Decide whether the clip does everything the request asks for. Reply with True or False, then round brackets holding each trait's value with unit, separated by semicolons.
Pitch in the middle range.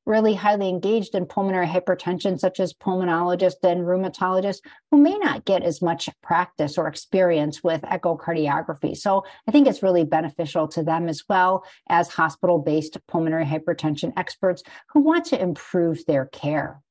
True (180 Hz)